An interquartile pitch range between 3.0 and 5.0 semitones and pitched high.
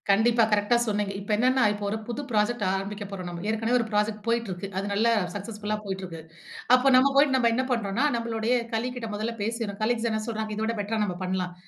No: narrow, 2.6 semitones; high, 220 Hz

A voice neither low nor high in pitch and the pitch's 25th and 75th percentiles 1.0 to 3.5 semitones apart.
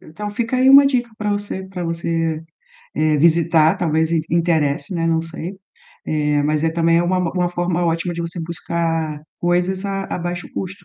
Yes: medium, 170 Hz; narrow, 2.4 semitones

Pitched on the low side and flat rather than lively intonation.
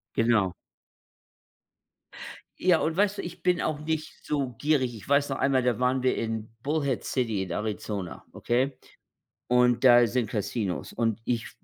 No: low, 125 Hz; average, 4.3 semitones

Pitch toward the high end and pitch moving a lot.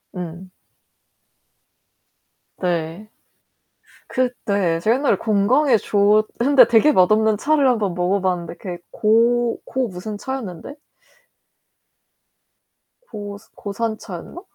No: high, 215 Hz; average, 4.7 semitones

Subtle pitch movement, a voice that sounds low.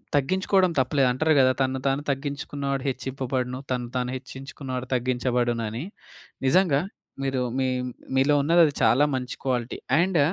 Yes: narrow, 2.1 semitones; low, 130 Hz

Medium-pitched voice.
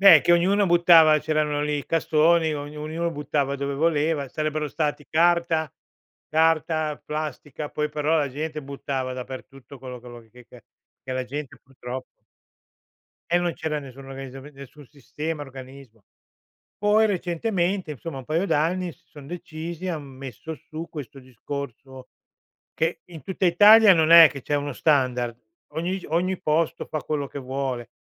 Yes: medium, 150 Hz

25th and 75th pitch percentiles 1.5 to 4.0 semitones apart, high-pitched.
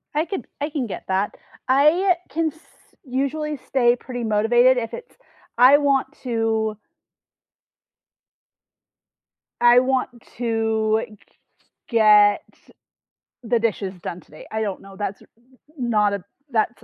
Yes: average, 3.7 semitones; high, 240 Hz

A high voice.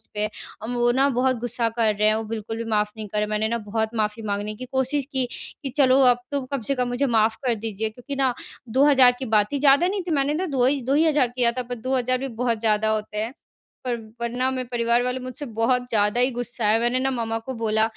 Yes: high, 245 Hz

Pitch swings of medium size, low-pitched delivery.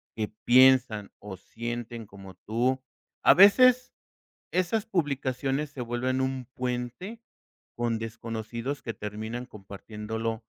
Yes: average, 3.0 semitones; low, 120 Hz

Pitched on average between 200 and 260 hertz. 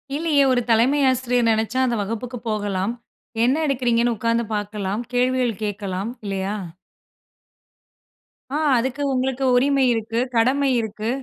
Yes: high, 235 Hz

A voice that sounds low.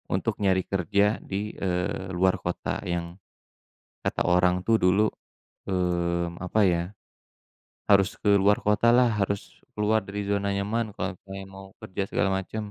Yes: very low, 95 Hz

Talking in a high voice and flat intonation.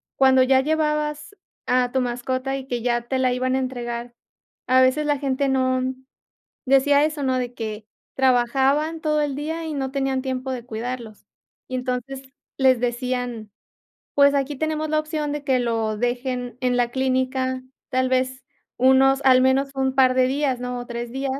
Yes: very high, 260 Hz; narrow, 1.7 semitones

